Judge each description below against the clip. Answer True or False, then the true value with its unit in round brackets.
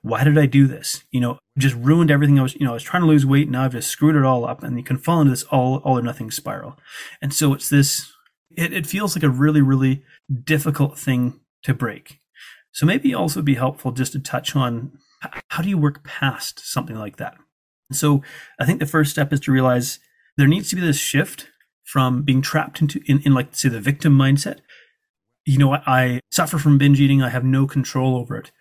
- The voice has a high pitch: False (140 Hz)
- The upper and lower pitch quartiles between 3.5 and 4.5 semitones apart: False (2.6 semitones)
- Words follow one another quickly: True (230 wpm)